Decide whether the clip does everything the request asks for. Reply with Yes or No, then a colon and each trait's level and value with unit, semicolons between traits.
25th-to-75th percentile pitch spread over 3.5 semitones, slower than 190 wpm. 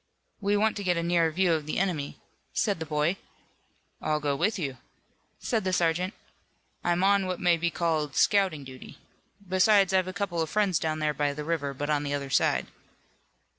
No: average, 4.0 semitones; average, 195 wpm